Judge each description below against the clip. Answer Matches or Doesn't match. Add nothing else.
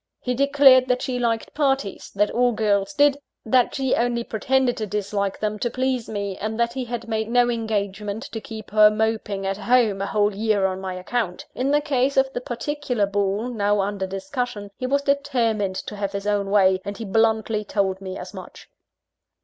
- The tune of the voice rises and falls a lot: Doesn't match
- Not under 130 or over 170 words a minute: Doesn't match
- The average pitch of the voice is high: Matches